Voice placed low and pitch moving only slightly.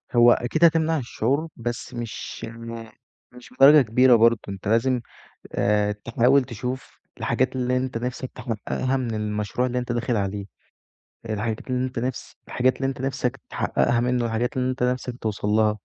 Yes: low, 120 Hz; narrow, 2.3 semitones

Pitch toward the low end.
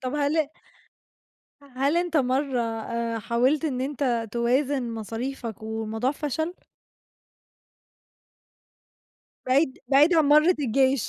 No: very high, 265 Hz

